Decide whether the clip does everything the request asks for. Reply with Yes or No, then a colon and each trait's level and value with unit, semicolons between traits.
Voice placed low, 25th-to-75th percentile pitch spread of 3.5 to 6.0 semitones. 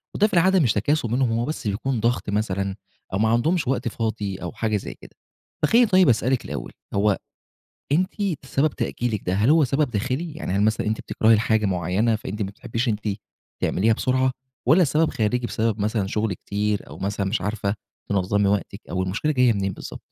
Yes: low, 110 Hz; average, 4.4 semitones